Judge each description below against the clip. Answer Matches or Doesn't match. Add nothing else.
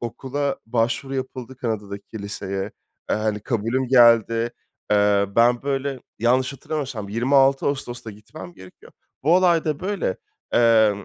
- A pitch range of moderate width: Matches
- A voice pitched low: Matches